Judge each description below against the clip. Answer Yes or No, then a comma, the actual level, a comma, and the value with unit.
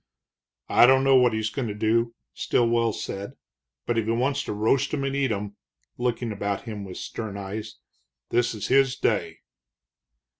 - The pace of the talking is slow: No, average, 175 wpm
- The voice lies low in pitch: Yes, low, 115 Hz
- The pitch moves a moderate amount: Yes, average, 3.2 semitones